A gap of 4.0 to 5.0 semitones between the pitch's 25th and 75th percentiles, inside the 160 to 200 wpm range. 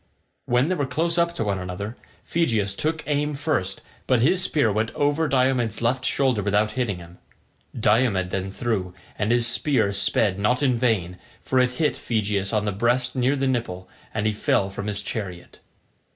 Yes: average, 4.7 semitones; average, 180 wpm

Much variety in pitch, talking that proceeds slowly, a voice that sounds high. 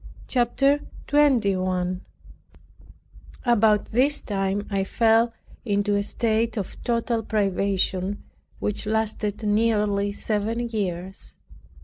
No: narrow, 2.6 semitones; slow, 90 wpm; high, 210 Hz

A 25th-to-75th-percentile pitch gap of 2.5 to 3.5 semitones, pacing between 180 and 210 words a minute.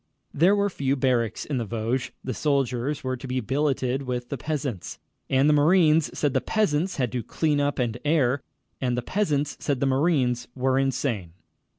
Yes: average, 3.1 semitones; average, 185 wpm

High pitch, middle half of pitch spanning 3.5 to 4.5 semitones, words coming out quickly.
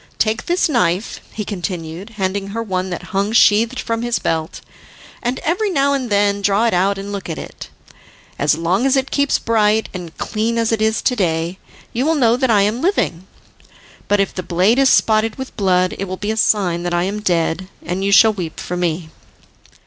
Yes: high, 205 Hz; average, 4.0 semitones; fast, 210 wpm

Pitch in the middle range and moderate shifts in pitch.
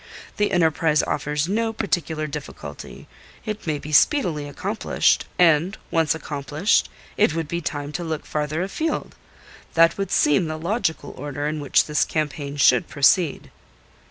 Yes: medium, 160 Hz; average, 3.4 semitones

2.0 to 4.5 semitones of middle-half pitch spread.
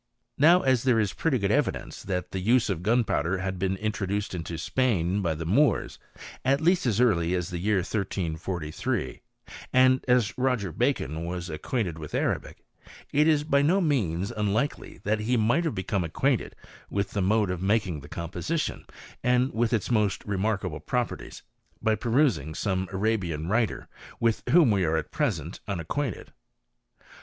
No: wide, 5.6 semitones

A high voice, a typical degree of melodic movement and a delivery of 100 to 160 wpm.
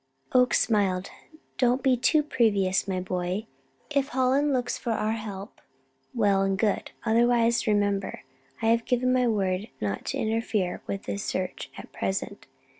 Yes: high, 220 Hz; average, 3.9 semitones; average, 150 wpm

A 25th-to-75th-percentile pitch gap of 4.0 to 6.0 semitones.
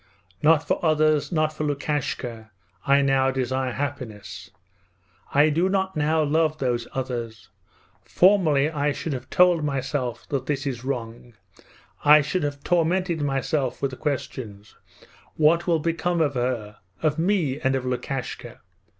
No: average, 3.3 semitones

